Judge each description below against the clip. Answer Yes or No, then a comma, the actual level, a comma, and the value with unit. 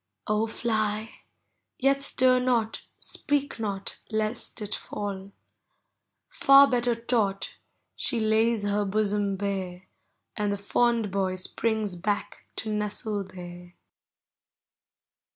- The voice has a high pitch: Yes, high, 215 Hz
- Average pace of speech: No, slow, 110 wpm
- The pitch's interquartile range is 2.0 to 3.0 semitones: Yes, narrow, 2.6 semitones